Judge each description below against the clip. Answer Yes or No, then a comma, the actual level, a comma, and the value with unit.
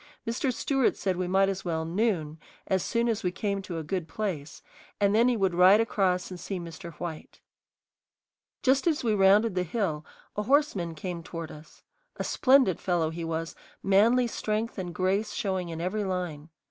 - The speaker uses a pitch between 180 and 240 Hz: Yes, high, 190 Hz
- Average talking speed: Yes, average, 185 wpm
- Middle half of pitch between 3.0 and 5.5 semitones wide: Yes, average, 4.1 semitones